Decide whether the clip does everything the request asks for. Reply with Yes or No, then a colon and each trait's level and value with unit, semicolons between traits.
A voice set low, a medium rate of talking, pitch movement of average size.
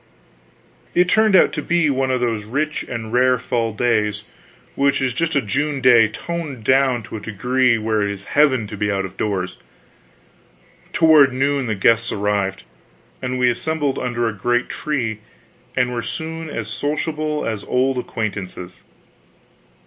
Yes: low, 125 Hz; average, 160 wpm; average, 4.6 semitones